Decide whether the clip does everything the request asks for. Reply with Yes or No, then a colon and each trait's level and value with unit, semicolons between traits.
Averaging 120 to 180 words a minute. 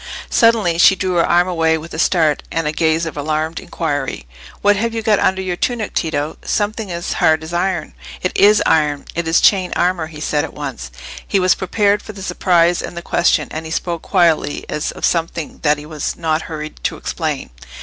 No: fast, 205 wpm